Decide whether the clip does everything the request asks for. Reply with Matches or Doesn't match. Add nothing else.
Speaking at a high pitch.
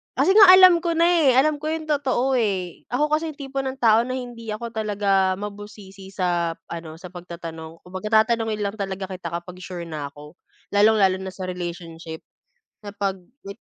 Matches